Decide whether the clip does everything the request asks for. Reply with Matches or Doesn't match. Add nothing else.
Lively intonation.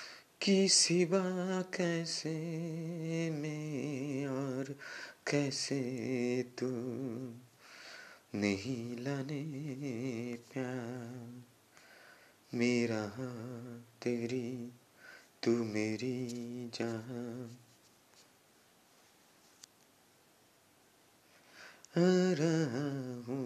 Doesn't match